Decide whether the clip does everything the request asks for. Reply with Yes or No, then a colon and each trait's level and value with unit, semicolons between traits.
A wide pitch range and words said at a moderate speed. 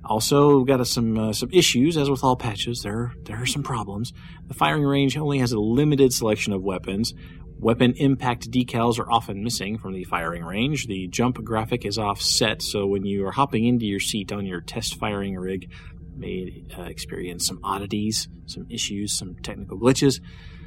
No: average, 4.1 semitones; average, 190 wpm